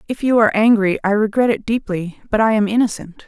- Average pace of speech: No, fast, 220 wpm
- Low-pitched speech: No, high, 215 Hz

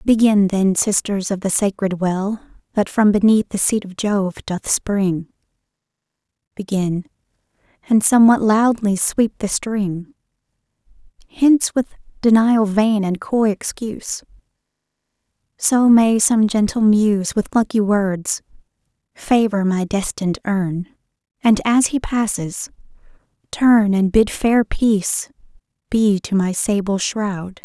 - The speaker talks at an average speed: No, slow, 120 wpm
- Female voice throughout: Yes, female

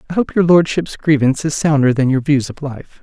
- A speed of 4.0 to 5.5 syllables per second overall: No, 5.7 syllables/s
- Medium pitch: Yes, medium, 145 Hz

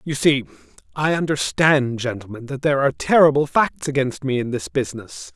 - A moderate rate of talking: Yes, average, 170 wpm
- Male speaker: Yes, male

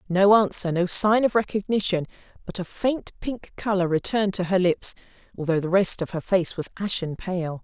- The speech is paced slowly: No, average, 190 wpm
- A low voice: No, high, 190 Hz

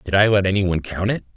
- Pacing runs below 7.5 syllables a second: No, 7.6 syllables/s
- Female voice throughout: No, male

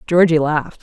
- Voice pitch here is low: No, medium, 155 Hz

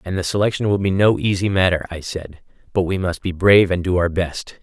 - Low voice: Yes, very low, 90 Hz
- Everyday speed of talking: No, fast, 245 wpm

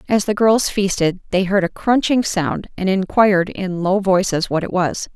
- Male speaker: No, female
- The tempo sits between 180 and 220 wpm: Yes, average, 200 wpm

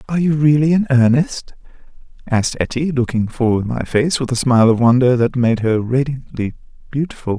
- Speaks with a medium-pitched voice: No, low, 130 Hz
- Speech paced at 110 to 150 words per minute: No, average, 180 wpm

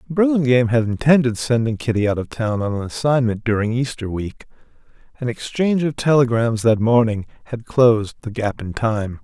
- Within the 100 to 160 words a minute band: No, average, 170 wpm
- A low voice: Yes, low, 120 Hz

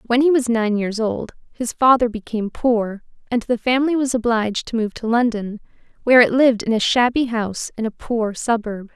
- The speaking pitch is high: Yes, high, 230 Hz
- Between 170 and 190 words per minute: No, average, 200 wpm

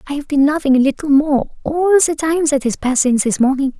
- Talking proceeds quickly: Yes, fast, 255 wpm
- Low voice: No, very high, 285 Hz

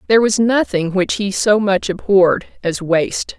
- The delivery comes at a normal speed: Yes, average, 175 wpm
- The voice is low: No, high, 195 Hz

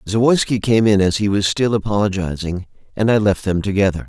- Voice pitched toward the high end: No, low, 105 Hz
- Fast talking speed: No, average, 190 wpm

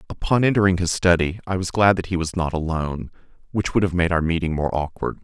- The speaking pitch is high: No, very low, 85 Hz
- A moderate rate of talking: No, fast, 230 wpm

